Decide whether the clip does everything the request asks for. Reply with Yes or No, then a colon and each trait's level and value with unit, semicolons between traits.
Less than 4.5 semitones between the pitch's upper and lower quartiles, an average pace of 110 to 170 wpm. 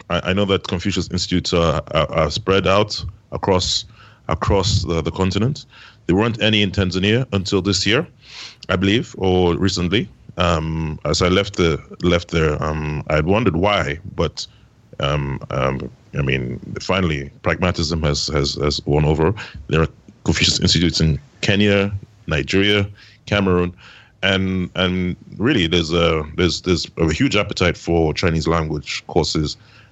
Yes: average, 3.9 semitones; average, 145 wpm